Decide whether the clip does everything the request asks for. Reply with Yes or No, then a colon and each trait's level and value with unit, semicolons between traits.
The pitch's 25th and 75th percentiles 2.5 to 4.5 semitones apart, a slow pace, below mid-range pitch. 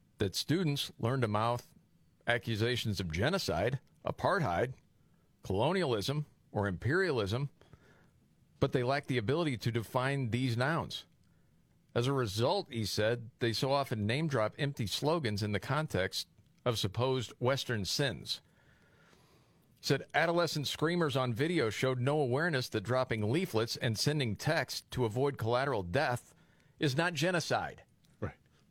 Yes: average, 4.2 semitones; slow, 125 wpm; low, 130 Hz